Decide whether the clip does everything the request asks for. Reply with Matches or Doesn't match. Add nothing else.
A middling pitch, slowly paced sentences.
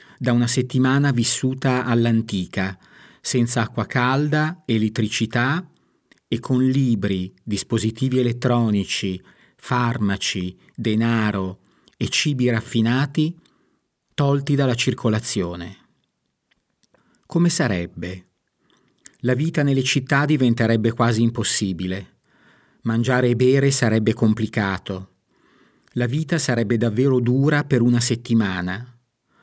Doesn't match